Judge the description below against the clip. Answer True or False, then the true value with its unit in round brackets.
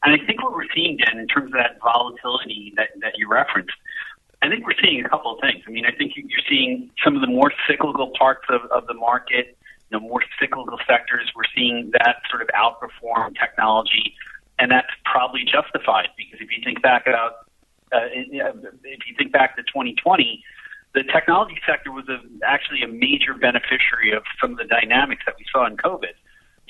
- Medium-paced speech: True (195 wpm)